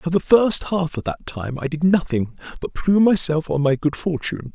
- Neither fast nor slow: No, fast, 225 wpm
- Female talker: No, male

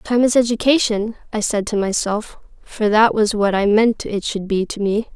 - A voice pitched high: Yes, high, 215 Hz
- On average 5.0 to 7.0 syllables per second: No, 4.7 syllables/s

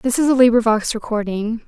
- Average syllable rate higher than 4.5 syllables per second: Yes, 5.7 syllables/s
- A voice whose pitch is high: Yes, high, 230 Hz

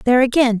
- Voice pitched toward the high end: Yes, very high, 250 Hz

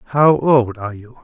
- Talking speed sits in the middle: Yes, average, 195 wpm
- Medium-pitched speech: No, low, 125 Hz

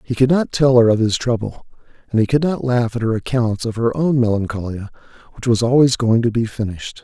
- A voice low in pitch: Yes, low, 120 Hz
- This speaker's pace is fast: Yes, fast, 230 wpm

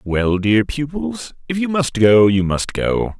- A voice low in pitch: Yes, low, 130 Hz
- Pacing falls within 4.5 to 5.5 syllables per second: No, 3.7 syllables/s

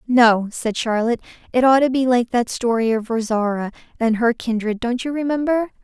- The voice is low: No, high, 240 Hz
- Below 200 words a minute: Yes, average, 185 wpm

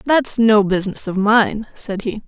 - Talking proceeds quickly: No, average, 185 wpm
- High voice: Yes, high, 215 Hz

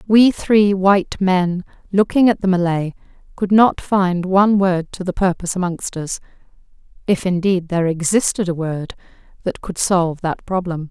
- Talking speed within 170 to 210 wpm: No, average, 155 wpm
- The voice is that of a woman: Yes, female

